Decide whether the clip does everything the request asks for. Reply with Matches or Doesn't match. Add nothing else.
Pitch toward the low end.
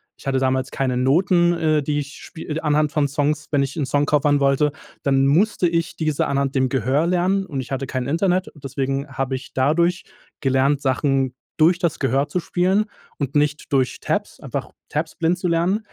Doesn't match